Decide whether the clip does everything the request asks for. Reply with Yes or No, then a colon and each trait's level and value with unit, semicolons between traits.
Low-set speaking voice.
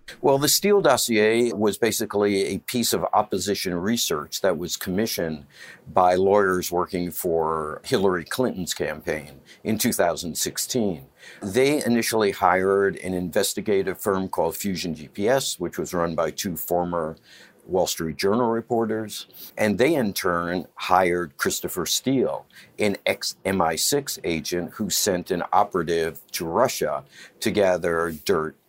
Yes: very low, 95 Hz